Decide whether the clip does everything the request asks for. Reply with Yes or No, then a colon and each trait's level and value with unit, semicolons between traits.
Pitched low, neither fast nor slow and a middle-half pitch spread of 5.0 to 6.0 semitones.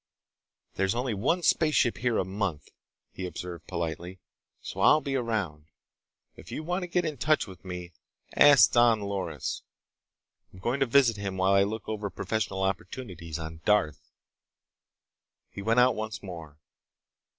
Yes: low, 100 Hz; average, 150 wpm; average, 5.3 semitones